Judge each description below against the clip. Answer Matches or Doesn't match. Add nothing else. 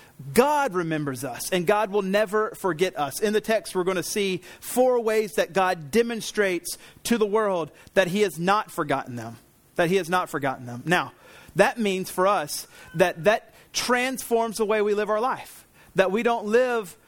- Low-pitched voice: Doesn't match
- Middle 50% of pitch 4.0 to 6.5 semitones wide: Matches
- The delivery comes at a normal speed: Matches